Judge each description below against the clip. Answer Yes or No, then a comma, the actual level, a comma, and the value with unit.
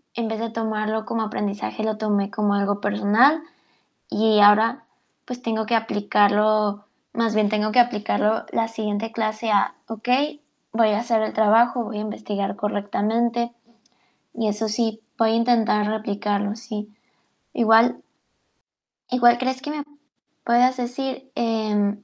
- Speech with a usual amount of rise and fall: No, narrow, 2.0 semitones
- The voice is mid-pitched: No, high, 220 Hz